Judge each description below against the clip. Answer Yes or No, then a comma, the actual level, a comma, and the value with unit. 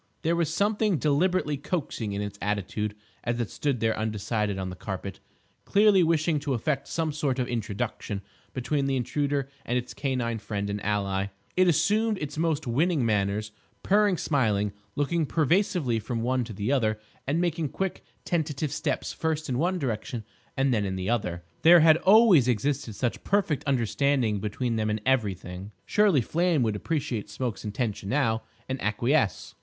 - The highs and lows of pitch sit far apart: Yes, wide, 6.8 semitones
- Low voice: Yes, low, 130 Hz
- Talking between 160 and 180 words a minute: Yes, average, 165 wpm